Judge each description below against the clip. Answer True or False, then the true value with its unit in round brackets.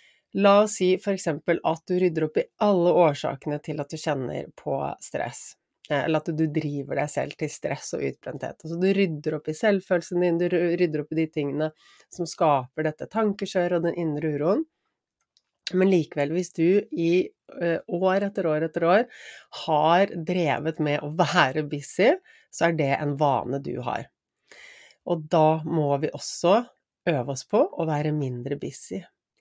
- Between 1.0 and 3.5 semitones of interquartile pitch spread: True (3.0 semitones)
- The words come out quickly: False (170 wpm)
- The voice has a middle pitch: True (165 Hz)